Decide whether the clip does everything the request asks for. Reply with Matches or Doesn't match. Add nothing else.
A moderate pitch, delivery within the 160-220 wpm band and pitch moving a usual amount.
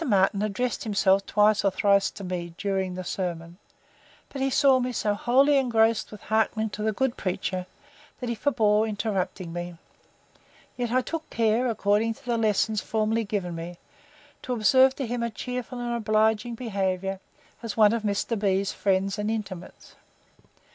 Doesn't match